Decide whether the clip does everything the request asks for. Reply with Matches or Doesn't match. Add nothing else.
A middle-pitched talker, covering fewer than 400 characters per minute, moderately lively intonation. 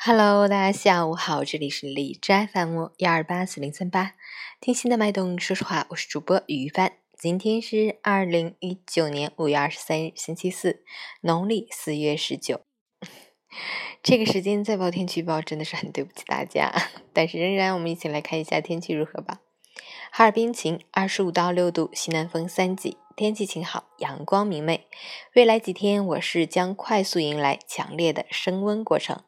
Matches